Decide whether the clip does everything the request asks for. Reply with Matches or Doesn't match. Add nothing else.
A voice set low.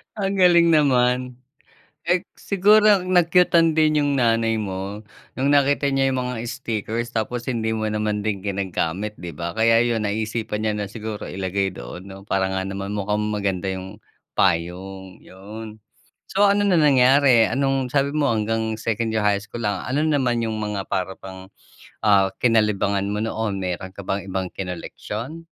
Matches